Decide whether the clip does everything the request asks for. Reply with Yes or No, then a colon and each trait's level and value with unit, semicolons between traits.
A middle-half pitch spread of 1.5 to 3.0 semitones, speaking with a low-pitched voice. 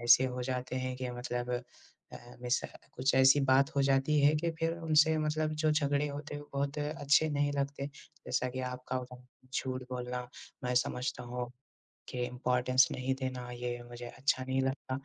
Yes: narrow, 2.4 semitones; low, 130 Hz